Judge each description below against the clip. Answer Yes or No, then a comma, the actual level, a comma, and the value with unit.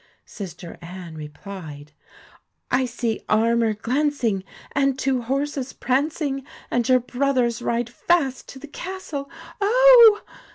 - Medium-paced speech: No, slow, 120 wpm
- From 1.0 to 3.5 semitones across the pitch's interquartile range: No, average, 4.6 semitones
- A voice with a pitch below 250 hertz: No, very high, 255 Hz